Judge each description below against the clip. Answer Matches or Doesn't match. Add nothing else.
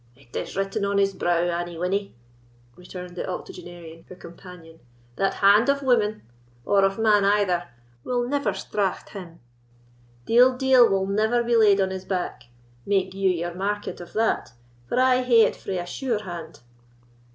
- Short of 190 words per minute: Matches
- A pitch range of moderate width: Matches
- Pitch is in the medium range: Doesn't match